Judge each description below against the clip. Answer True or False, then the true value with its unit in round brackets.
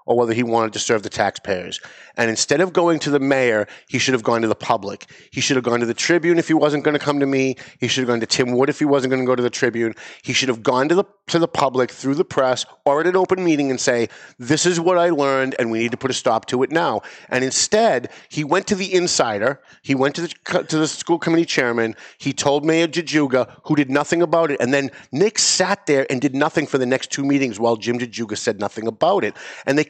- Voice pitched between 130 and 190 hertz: True (140 Hz)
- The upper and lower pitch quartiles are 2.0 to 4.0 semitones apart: False (4.8 semitones)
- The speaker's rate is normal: False (270 wpm)